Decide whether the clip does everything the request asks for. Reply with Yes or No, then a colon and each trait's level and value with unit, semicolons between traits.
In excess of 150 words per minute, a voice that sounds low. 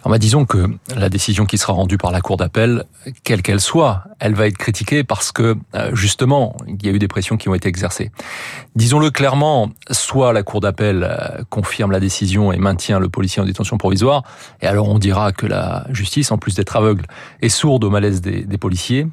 Yes: average, 210 wpm; low, 105 Hz